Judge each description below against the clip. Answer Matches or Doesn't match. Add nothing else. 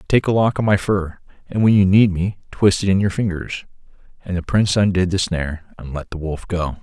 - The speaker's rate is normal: Doesn't match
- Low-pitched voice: Matches